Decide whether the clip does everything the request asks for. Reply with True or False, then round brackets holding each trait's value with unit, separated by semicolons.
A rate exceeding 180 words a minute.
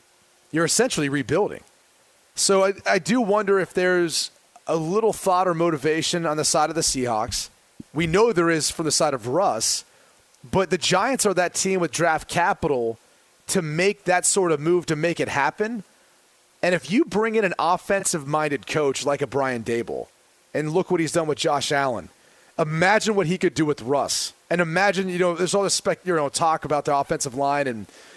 True (190 wpm)